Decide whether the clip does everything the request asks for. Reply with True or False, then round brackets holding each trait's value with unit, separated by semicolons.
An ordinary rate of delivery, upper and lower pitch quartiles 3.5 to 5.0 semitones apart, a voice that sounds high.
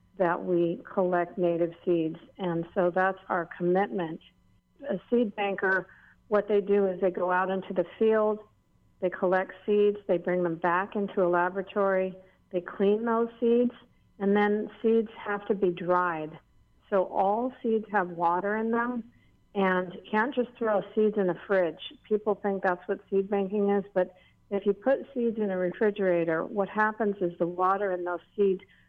False (170 wpm; 2.8 semitones; 195 Hz)